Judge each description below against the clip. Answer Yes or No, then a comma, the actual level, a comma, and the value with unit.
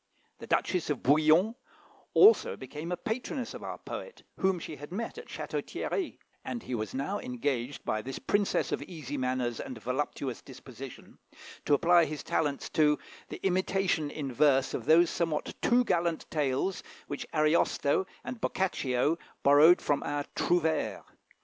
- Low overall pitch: No, medium, 155 Hz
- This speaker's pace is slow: No, average, 155 wpm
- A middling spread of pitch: Yes, average, 4.9 semitones